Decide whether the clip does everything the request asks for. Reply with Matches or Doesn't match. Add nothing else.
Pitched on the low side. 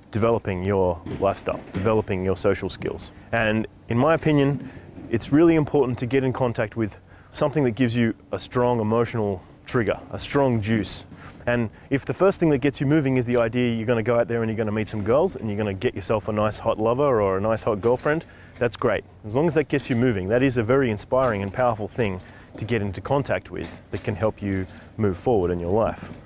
Matches